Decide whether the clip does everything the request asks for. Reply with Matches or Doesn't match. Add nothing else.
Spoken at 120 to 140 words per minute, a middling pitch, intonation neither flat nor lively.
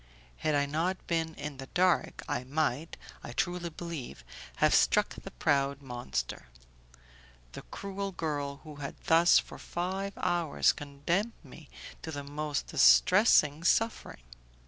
Matches